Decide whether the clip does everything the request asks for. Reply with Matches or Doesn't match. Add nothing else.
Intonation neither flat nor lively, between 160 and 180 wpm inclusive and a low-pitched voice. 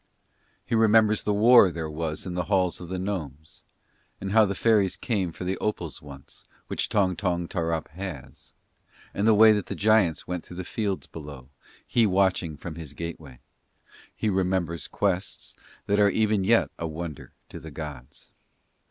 Matches